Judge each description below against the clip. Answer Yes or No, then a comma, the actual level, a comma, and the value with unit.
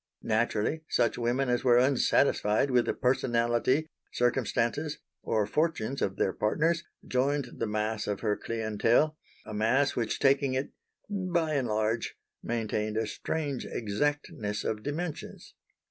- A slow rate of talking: Yes, slow, 130 wpm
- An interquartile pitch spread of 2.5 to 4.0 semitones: No, average, 4.7 semitones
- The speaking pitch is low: Yes, low, 120 Hz